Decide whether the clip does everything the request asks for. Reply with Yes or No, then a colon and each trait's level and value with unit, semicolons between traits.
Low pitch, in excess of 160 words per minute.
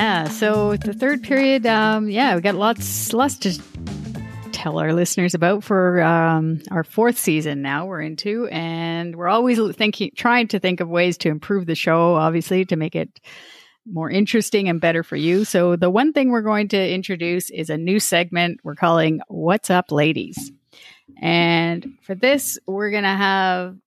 No: medium, 180 Hz; average, 175 wpm